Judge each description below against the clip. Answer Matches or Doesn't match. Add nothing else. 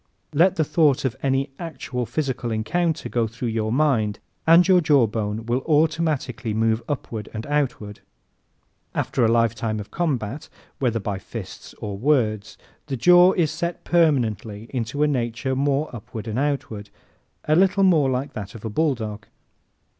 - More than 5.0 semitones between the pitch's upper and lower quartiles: Matches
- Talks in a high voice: Doesn't match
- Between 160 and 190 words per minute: Doesn't match